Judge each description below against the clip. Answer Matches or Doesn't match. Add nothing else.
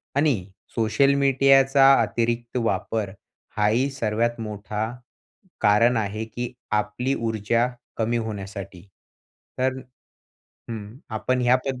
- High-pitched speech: Doesn't match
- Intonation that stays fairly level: Doesn't match